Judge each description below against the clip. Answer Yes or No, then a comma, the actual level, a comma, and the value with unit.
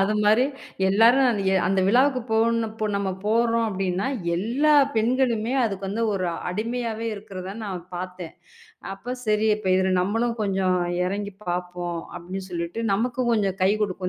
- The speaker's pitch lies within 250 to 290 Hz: No, high, 205 Hz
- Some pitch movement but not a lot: Yes, average, 3.5 semitones